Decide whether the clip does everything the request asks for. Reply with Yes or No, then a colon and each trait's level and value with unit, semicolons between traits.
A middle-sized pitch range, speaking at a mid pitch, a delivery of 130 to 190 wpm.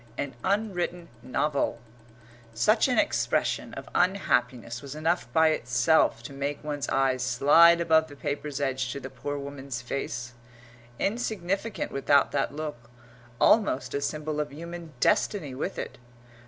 Yes: average, 4.2 semitones; medium, 145 Hz; average, 140 wpm